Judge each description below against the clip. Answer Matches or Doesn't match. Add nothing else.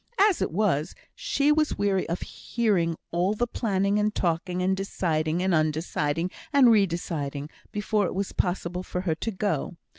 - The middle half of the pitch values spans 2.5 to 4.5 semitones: Matches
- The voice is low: Doesn't match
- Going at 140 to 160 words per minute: Doesn't match